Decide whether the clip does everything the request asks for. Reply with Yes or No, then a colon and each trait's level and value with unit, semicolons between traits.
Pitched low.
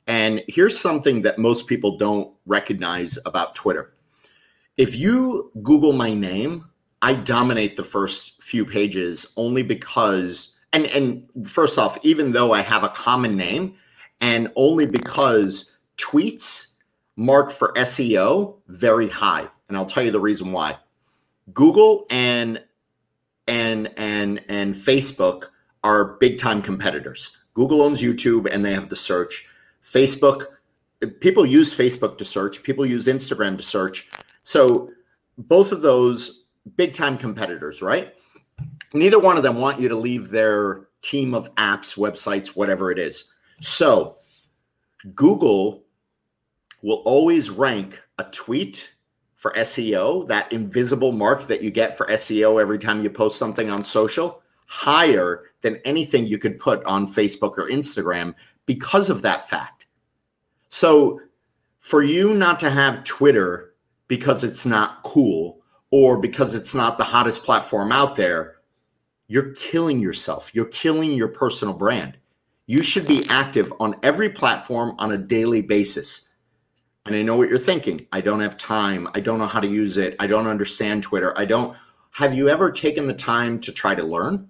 Yes: low, 115 Hz